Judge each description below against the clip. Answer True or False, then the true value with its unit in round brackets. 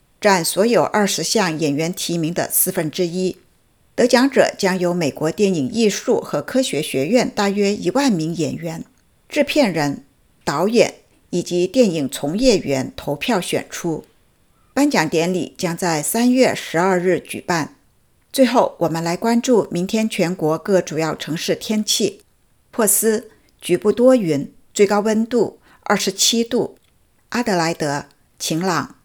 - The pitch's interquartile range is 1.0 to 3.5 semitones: False (5.2 semitones)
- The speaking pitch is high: True (195 Hz)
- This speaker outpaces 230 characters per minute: False (215 characters per minute)